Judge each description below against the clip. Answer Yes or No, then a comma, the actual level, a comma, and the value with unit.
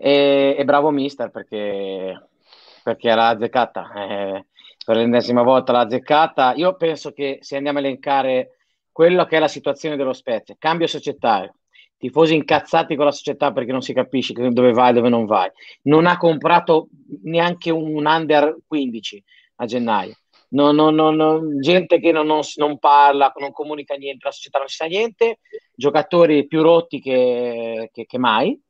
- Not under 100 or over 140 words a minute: No, average, 165 wpm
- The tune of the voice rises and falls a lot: No, average, 3.8 semitones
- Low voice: No, medium, 145 Hz